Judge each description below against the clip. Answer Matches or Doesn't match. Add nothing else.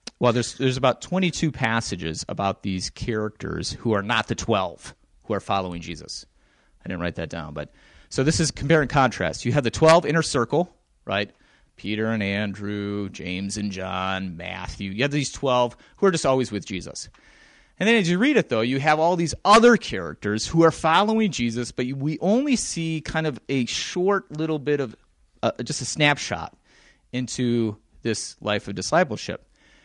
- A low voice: Matches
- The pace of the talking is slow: Doesn't match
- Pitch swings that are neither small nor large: Doesn't match